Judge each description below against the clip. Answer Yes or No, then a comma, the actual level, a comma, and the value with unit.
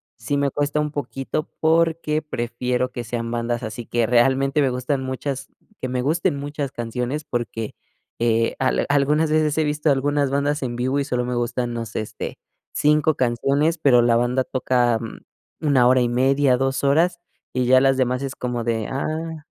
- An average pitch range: Yes, average, 3.1 semitones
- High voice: No, low, 130 Hz